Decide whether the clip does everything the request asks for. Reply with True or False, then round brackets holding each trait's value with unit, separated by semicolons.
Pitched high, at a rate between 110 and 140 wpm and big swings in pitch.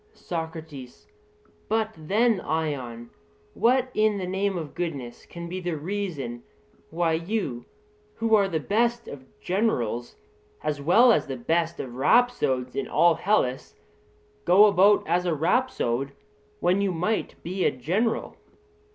False (170 Hz; 135 wpm; 6.4 semitones)